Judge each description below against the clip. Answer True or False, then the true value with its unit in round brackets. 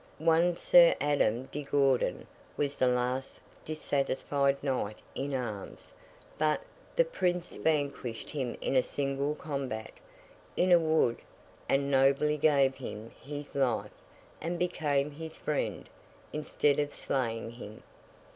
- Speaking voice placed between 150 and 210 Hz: False (140 Hz)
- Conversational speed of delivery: False (120 wpm)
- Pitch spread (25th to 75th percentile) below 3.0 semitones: True (2.6 semitones)